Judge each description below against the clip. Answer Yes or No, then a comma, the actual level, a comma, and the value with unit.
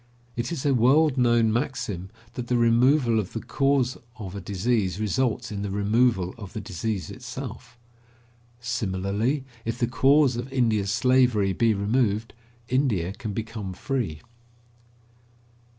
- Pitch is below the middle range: Yes, low, 115 Hz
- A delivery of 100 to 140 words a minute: Yes, slow, 135 wpm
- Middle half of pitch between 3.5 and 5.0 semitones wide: Yes, average, 3.9 semitones